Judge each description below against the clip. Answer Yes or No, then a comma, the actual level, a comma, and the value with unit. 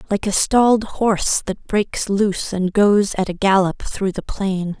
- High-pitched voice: Yes, high, 200 Hz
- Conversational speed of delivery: Yes, average, 190 wpm